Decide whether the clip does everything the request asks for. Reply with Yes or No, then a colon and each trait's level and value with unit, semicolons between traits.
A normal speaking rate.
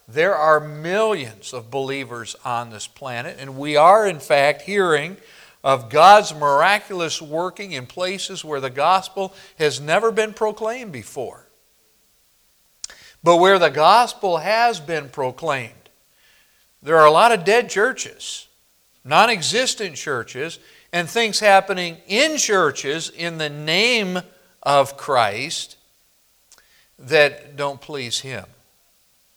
No: slow, 120 wpm